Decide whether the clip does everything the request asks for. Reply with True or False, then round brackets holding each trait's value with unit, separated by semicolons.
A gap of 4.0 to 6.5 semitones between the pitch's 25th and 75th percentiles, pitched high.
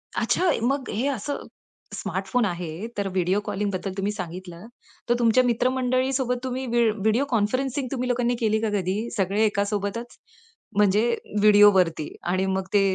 True (4.3 semitones; 210 Hz)